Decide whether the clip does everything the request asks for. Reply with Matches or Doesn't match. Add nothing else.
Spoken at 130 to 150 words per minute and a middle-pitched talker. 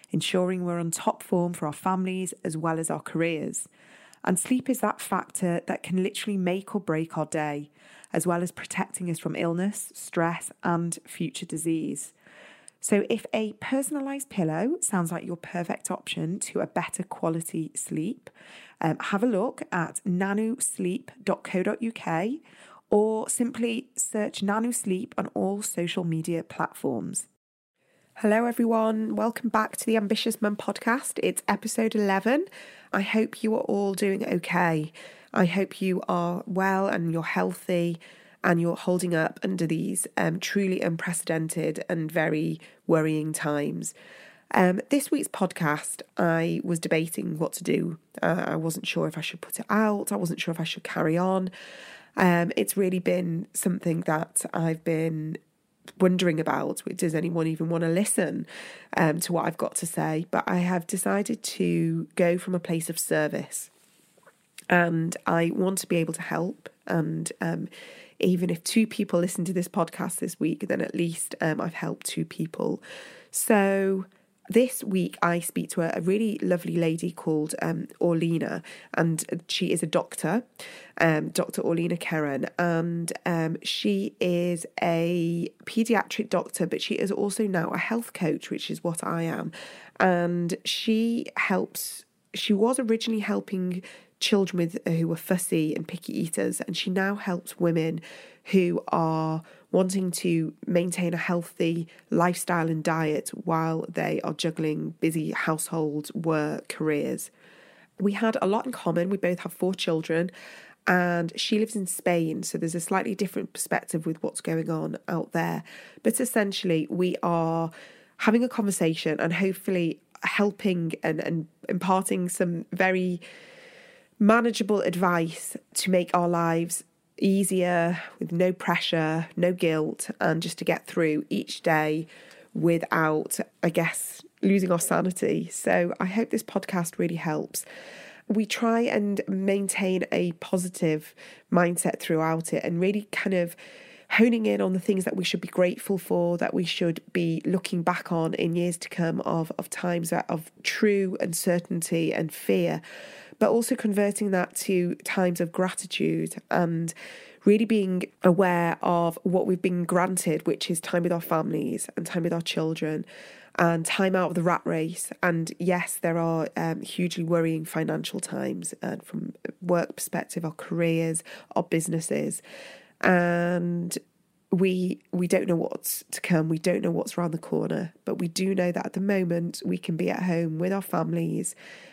Doesn't match